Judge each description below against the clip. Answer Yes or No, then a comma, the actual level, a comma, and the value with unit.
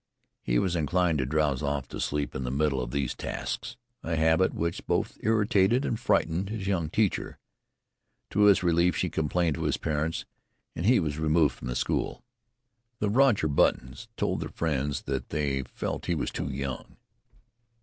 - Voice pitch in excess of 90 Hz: No, very low, 80 Hz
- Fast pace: No, average, 175 wpm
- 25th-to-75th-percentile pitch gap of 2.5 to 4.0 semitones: No, average, 4.8 semitones